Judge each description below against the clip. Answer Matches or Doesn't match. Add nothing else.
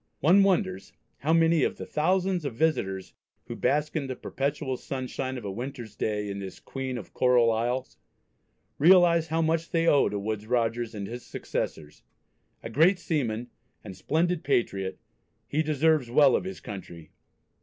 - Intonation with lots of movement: Matches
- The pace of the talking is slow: Doesn't match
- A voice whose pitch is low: Matches